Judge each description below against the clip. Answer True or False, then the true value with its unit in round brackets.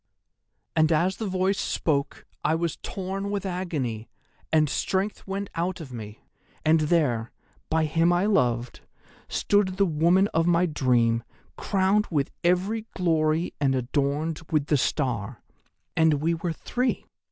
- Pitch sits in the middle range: True (165 Hz)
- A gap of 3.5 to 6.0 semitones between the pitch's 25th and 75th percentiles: True (4.8 semitones)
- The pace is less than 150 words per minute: True (140 wpm)